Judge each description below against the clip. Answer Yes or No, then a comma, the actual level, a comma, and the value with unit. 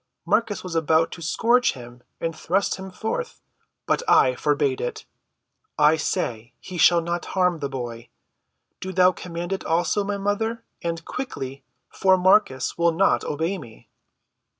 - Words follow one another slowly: No, average, 150 wpm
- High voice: No, medium, 175 Hz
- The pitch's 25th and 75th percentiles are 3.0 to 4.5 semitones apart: Yes, average, 4.1 semitones